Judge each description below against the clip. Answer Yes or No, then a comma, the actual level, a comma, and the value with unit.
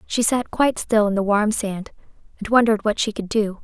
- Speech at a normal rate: No, fast, 230 wpm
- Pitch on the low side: No, high, 215 Hz